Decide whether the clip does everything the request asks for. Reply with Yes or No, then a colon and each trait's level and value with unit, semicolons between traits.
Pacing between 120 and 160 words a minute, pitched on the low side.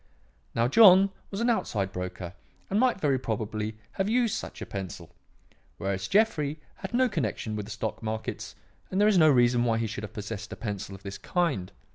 No: average, 195 wpm; low, 115 Hz